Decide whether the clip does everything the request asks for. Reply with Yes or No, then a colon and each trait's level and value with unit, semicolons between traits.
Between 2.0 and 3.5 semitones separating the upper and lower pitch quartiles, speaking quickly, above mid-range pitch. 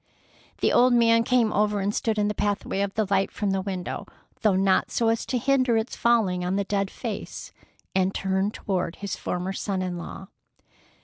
No: average, 2.9 semitones; average, 190 wpm; high, 200 Hz